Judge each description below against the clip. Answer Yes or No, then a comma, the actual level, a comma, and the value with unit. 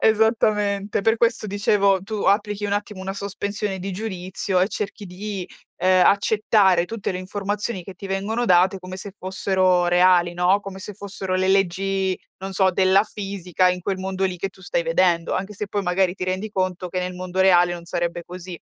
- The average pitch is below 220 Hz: Yes, high, 190 Hz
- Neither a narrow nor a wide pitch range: No, narrow, 1.8 semitones